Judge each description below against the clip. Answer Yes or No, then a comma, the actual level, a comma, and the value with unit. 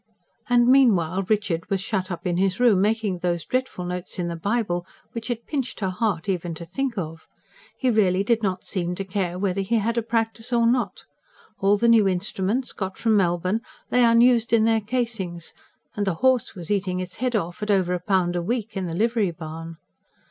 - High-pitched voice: Yes, high, 200 Hz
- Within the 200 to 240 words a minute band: Yes, fast, 205 wpm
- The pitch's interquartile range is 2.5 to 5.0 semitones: Yes, average, 4.3 semitones